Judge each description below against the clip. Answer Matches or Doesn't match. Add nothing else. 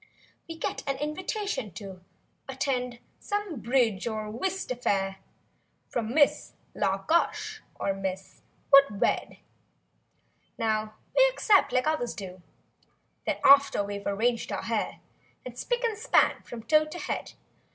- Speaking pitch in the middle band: Doesn't match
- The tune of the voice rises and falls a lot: Matches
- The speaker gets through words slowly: Matches